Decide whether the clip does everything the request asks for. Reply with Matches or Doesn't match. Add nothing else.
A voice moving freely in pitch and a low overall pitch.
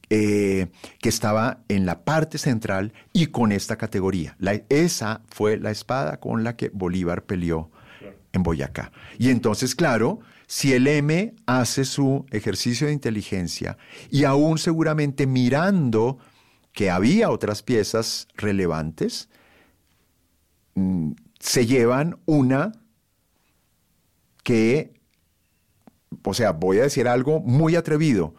Matches